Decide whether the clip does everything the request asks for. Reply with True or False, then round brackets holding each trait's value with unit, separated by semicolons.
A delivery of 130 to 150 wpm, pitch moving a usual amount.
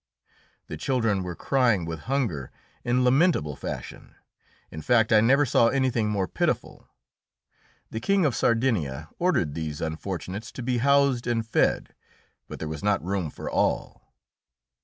False (145 wpm; 7.3 semitones)